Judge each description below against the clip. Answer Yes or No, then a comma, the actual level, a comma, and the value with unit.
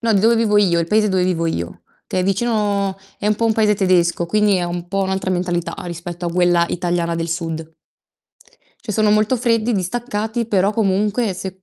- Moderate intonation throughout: Yes, average, 3.4 semitones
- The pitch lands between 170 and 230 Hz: Yes, high, 190 Hz